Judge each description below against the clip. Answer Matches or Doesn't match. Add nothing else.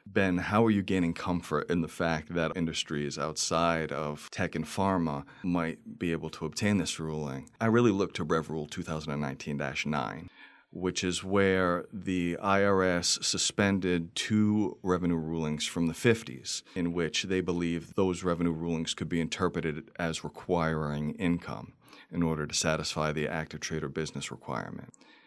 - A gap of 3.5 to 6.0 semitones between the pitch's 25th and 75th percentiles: Doesn't match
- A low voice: Matches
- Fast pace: Doesn't match